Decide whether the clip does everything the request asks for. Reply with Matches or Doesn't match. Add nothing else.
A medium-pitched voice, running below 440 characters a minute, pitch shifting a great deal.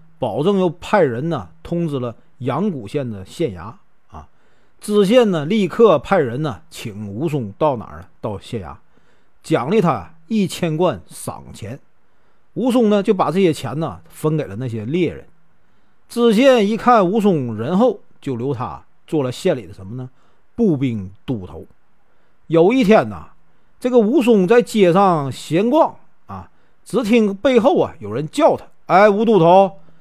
Matches